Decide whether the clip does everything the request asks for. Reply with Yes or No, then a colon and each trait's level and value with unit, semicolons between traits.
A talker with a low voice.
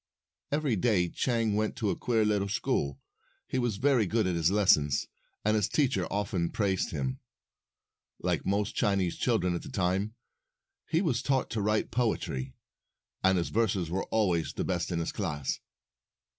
Yes: low, 100 Hz